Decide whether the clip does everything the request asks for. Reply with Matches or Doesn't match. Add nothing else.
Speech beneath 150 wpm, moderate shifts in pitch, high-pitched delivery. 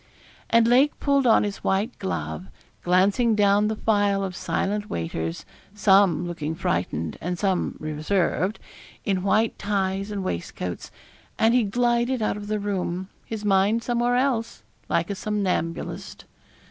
Matches